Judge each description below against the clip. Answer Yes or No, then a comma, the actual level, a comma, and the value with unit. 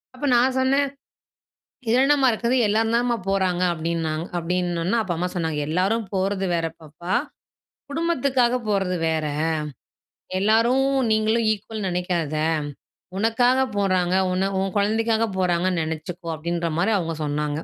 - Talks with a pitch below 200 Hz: Yes, high, 190 Hz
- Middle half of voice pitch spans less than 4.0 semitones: No, average, 5.0 semitones